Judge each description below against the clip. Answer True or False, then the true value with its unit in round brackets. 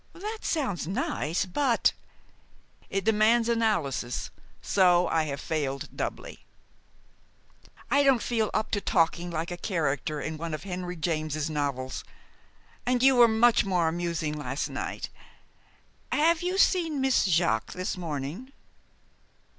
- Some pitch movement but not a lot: False (7.3 semitones)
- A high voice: False (180 Hz)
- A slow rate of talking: True (130 wpm)